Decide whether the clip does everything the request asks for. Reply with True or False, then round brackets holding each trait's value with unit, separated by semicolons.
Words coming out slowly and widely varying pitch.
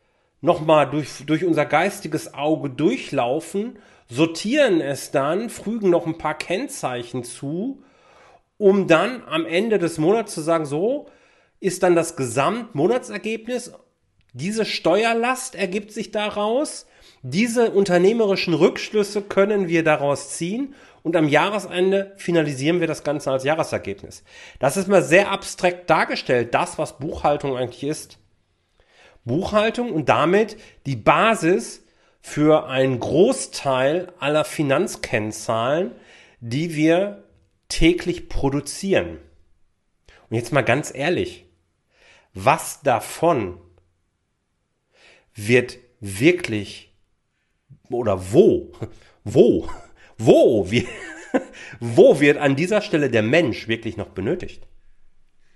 True (105 wpm; 7.6 semitones)